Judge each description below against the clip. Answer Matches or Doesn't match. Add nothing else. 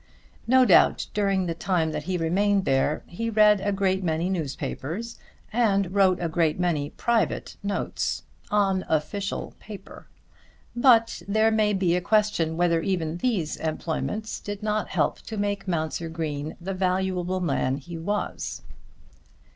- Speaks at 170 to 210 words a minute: Doesn't match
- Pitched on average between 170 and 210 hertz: Matches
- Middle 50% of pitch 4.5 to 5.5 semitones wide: Doesn't match